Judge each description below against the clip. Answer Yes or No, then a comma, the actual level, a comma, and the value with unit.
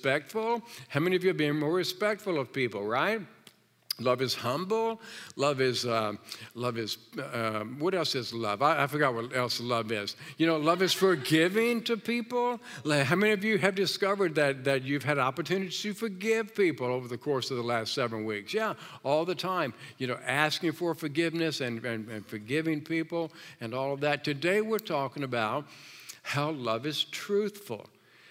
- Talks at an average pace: Yes, average, 185 wpm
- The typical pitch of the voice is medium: Yes, medium, 150 Hz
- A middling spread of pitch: No, wide, 6.8 semitones